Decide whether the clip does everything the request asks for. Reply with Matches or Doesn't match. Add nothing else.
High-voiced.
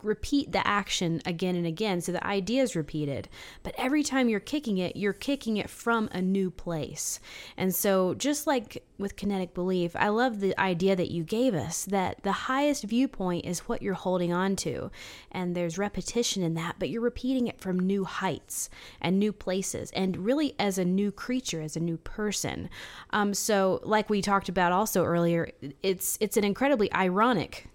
Matches